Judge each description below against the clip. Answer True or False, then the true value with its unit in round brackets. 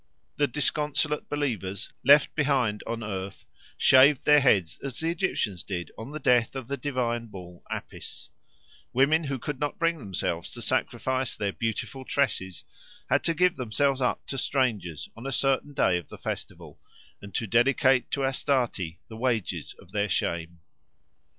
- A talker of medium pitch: False (125 Hz)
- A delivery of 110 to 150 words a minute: False (160 wpm)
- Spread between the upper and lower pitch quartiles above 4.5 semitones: True (5.5 semitones)